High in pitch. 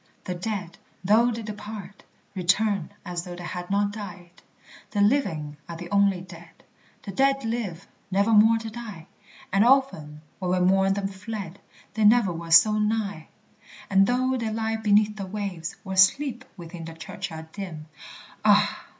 Yes: high, 200 Hz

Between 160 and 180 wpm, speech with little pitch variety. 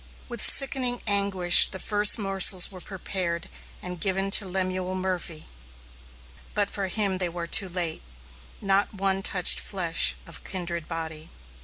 No: average, 140 wpm; narrow, 2.1 semitones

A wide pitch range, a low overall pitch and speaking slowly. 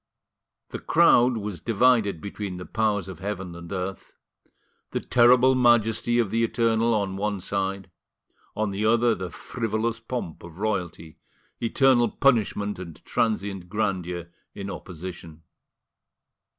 No: average, 3.8 semitones; low, 105 Hz; slow, 125 wpm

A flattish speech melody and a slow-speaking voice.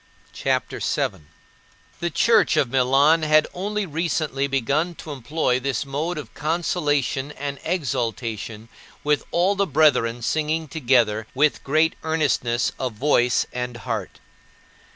No: average, 4.4 semitones; slow, 130 wpm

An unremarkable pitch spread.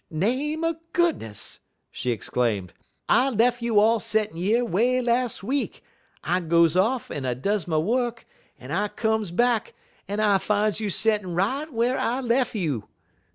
No: wide, 5.7 semitones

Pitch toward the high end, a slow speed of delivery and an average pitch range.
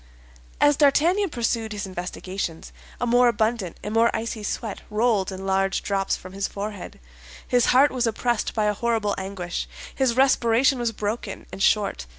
No: high, 220 Hz; average, 165 wpm; average, 3.6 semitones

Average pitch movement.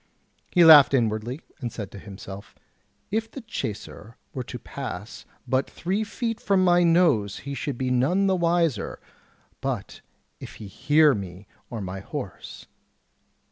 No: wide, 8.6 semitones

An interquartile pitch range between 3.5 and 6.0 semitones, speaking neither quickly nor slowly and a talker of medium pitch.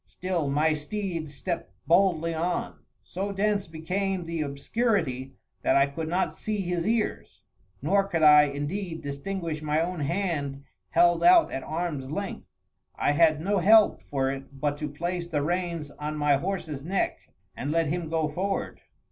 Yes: average, 4.1 semitones; average, 160 wpm; medium, 165 Hz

